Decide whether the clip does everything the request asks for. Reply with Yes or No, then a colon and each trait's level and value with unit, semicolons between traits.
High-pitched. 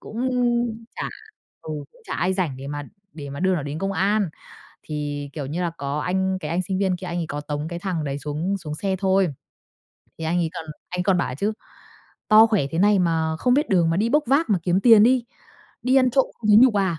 No: medium, 180 Hz